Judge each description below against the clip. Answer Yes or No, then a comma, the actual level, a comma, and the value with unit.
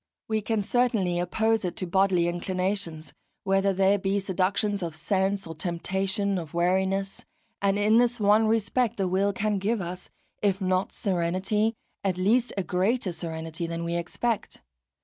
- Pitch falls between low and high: No, high, 195 Hz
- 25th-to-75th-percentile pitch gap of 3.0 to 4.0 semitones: No, narrow, 2.6 semitones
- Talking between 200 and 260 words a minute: No, average, 155 wpm